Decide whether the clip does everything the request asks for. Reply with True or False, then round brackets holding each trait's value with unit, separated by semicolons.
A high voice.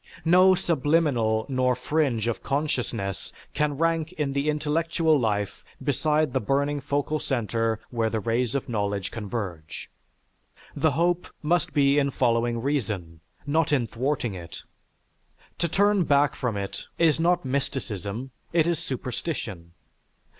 False (135 Hz)